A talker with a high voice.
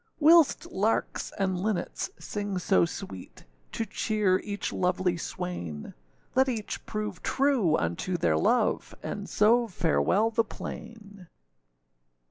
Yes: high, 200 Hz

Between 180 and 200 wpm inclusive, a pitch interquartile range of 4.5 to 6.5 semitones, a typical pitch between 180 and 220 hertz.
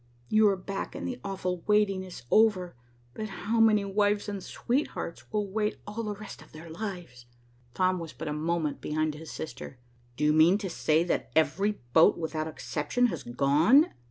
Yes: average, 185 wpm; average, 4.8 semitones; medium, 185 Hz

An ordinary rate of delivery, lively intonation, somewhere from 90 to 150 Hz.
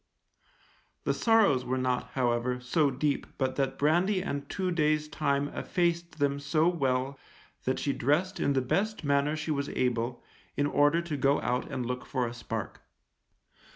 No: average, 165 wpm; average, 3.6 semitones; medium, 140 Hz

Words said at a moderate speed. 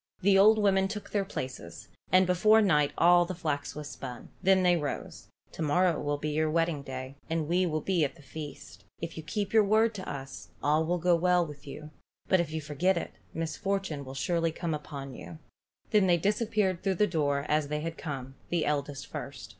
No: fast, 210 wpm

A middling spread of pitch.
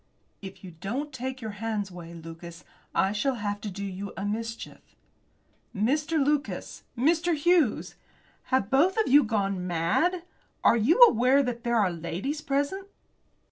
No: wide, 6.5 semitones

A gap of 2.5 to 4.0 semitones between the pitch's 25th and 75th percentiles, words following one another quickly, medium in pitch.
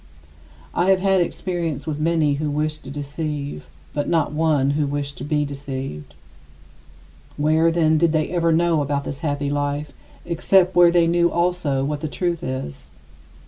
No: average, 2.9 semitones; average, 165 wpm; medium, 150 Hz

